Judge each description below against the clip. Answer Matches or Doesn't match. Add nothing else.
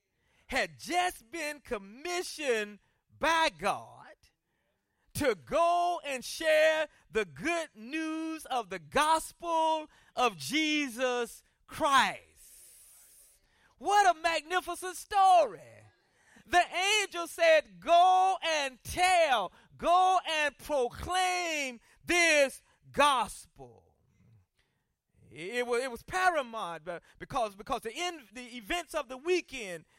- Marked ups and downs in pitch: Matches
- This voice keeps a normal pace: Doesn't match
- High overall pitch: Matches